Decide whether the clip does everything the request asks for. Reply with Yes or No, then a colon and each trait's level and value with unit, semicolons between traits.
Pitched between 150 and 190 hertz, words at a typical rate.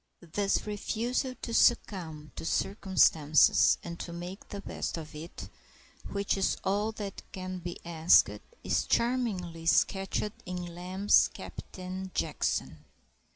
No: medium, 185 Hz; slow, 120 wpm